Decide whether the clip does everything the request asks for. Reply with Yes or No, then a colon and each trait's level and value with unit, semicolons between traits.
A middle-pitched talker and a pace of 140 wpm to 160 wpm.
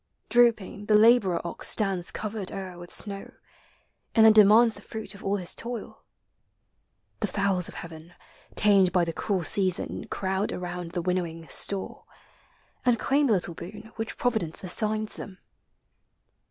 No: high, 195 Hz; average, 155 wpm